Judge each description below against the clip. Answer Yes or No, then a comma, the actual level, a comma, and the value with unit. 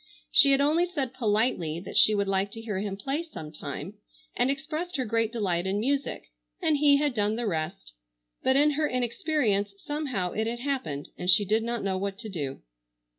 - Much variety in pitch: Yes, wide, 6.2 semitones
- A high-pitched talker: Yes, high, 225 Hz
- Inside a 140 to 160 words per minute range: No, average, 195 wpm